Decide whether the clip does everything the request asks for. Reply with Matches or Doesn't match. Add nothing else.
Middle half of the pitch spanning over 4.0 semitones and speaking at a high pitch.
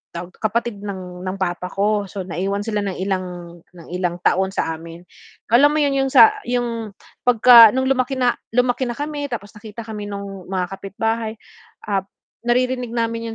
Matches